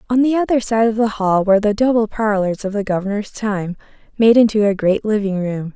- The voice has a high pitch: Yes, high, 210 Hz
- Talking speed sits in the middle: No, fast, 220 wpm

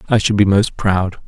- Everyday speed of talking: No, fast, 235 wpm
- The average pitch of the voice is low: Yes, low, 100 Hz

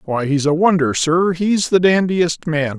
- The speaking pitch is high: No, medium, 165 Hz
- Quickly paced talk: No, average, 195 wpm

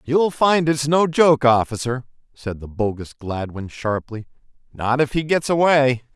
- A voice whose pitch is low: Yes, low, 130 Hz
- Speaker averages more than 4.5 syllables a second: No, 4.3 syllables/s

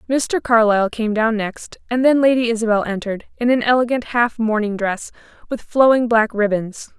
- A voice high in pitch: Yes, high, 230 Hz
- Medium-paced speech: Yes, average, 170 wpm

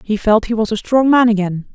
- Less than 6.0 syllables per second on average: Yes, 5.6 syllables/s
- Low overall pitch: No, high, 220 Hz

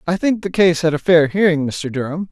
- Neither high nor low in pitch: Yes, medium, 165 Hz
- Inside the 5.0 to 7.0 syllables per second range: Yes, 5.5 syllables/s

